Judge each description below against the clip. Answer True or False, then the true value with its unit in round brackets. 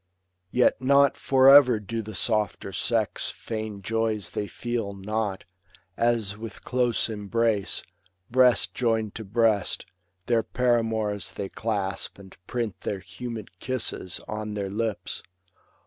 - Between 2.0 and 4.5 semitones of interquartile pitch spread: True (2.7 semitones)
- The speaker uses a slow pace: True (125 wpm)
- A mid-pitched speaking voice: False (110 Hz)